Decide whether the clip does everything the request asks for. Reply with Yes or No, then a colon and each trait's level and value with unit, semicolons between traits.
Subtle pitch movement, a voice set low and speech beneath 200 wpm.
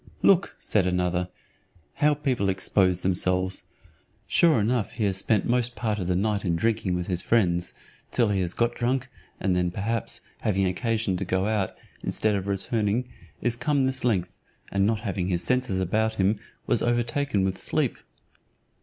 No: average, 4.1 semitones; low, 100 Hz; average, 170 wpm